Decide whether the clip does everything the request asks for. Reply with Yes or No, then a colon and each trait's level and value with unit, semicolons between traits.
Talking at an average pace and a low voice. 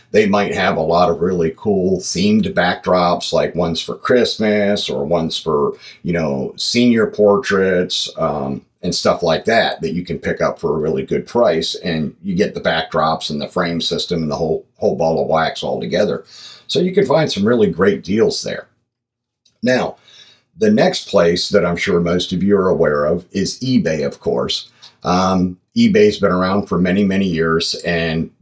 Yes: average, 190 wpm; very low, 95 Hz